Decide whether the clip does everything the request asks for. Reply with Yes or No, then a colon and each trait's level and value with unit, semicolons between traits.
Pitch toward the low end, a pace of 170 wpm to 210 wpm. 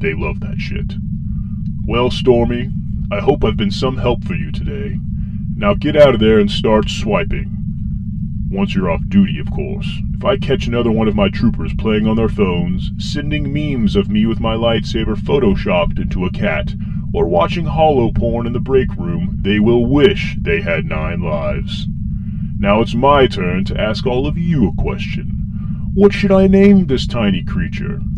Yes: low, 115 Hz; average, 180 wpm